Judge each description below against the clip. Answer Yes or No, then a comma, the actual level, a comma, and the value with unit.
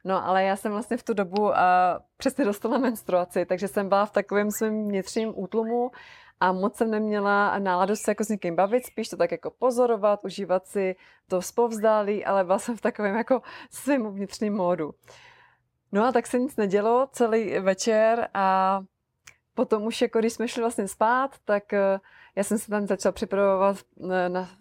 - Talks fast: Yes, fast, 180 wpm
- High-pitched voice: Yes, high, 210 Hz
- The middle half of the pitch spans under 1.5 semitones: No, average, 2.9 semitones